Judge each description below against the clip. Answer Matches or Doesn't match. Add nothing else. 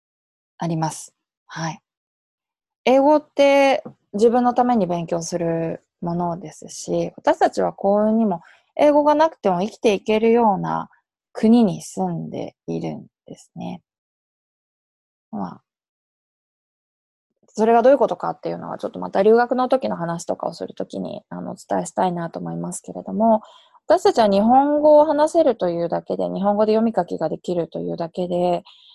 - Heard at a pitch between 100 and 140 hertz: Doesn't match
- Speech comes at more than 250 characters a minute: Matches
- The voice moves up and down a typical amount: Doesn't match